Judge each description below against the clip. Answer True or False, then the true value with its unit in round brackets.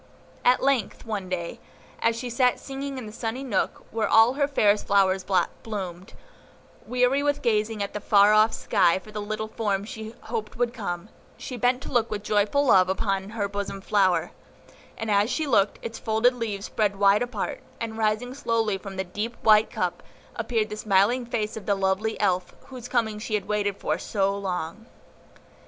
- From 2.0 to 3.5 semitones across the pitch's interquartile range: True (2.9 semitones)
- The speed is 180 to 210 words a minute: True (185 wpm)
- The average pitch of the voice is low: False (215 Hz)